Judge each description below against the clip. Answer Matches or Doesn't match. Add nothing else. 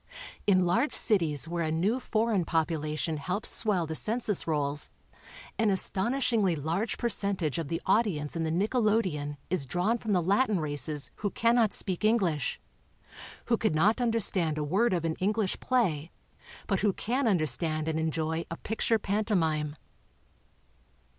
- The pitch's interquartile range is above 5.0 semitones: Matches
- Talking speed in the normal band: Matches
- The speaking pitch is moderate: Matches